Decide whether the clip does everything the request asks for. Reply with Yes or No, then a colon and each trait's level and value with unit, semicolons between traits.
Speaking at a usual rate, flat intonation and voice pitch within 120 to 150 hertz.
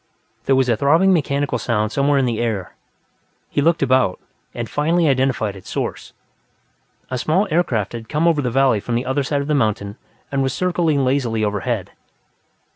No: average, 180 wpm; average, 4.1 semitones; low, 135 Hz